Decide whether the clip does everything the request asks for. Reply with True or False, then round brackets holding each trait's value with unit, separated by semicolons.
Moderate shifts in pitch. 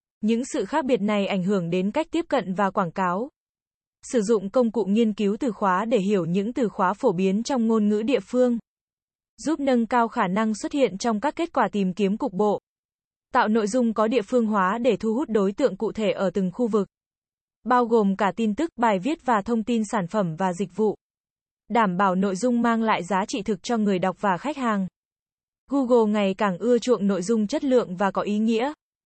True (3.6 semitones)